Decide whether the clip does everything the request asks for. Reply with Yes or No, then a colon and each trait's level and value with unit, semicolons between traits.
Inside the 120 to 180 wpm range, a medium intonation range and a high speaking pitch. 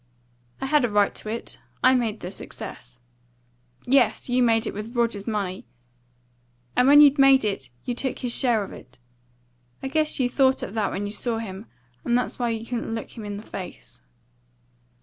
No: average, 190 wpm; average, 3.6 semitones; high, 230 Hz